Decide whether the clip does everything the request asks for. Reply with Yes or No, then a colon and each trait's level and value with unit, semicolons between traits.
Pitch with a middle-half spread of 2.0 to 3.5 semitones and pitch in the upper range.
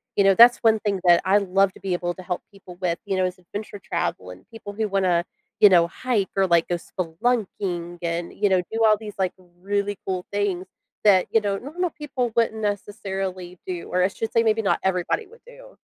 Yes: average, 3.1 semitones; high, 195 Hz